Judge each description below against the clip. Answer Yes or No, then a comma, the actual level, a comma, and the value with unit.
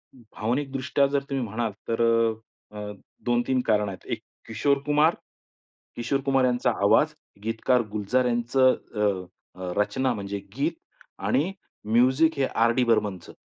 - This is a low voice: Yes, low, 120 Hz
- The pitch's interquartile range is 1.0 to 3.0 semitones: No, average, 3.6 semitones